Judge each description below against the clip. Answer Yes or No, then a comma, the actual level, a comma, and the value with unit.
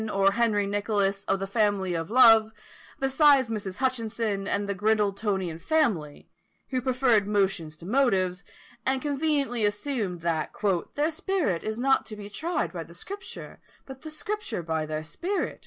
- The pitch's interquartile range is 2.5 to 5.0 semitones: No, wide, 5.4 semitones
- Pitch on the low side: No, high, 210 Hz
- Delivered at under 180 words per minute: Yes, average, 155 wpm